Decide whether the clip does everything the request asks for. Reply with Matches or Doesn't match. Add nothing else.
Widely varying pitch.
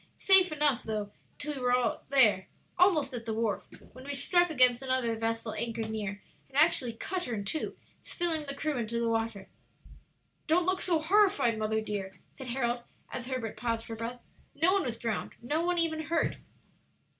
Matches